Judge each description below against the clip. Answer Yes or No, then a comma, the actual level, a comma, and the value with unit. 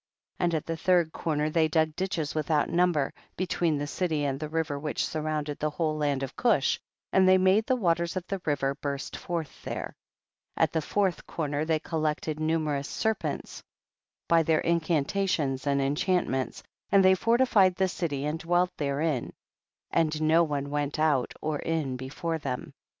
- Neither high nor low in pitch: Yes, medium, 155 Hz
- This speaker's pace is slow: No, average, 175 wpm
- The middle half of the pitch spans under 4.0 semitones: Yes, average, 3.1 semitones